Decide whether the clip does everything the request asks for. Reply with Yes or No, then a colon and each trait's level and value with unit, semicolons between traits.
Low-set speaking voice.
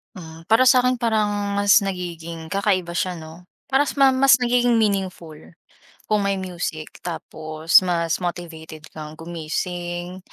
No: medium, 180 Hz